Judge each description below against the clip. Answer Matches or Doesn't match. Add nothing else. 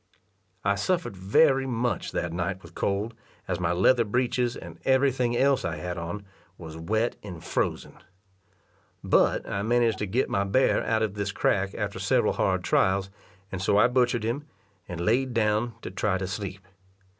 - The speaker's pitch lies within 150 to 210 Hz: Doesn't match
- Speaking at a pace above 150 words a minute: Matches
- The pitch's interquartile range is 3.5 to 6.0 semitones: Matches